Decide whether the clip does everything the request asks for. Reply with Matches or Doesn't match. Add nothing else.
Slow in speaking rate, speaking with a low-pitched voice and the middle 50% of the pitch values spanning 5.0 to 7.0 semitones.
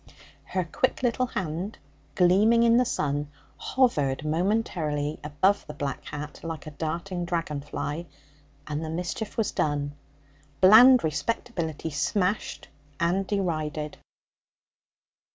Doesn't match